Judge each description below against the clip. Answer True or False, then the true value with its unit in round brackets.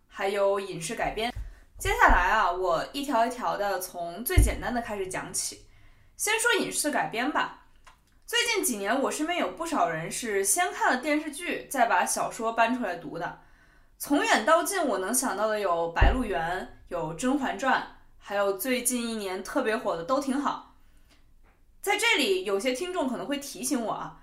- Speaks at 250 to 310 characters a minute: True (255 characters per minute)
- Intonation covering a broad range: True (7.7 semitones)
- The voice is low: False (245 Hz)